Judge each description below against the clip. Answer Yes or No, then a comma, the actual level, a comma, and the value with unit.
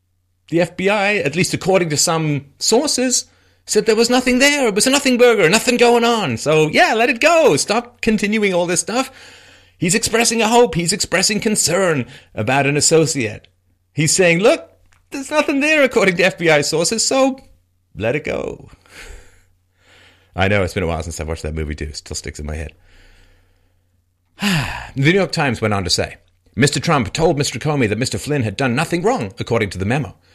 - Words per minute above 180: Yes, average, 190 wpm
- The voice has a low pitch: No, medium, 150 Hz